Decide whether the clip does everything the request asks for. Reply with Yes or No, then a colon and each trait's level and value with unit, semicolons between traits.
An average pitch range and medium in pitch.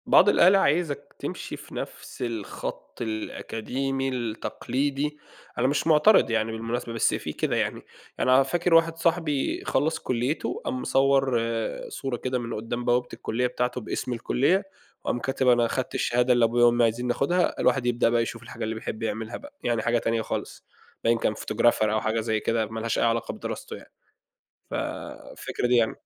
No: average, 3.0 semitones; low, 120 Hz